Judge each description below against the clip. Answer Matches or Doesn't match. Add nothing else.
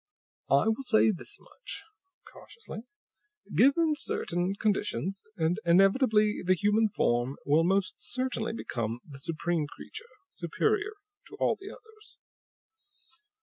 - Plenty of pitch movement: Matches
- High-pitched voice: Matches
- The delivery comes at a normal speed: Doesn't match